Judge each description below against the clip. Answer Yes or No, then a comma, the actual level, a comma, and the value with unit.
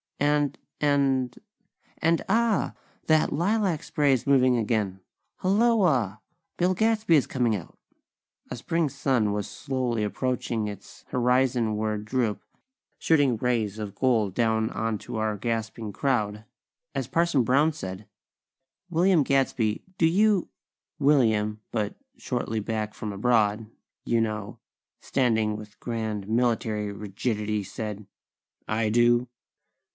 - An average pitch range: Yes, average, 4.7 semitones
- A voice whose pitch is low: Yes, low, 120 Hz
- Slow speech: Yes, slow, 115 wpm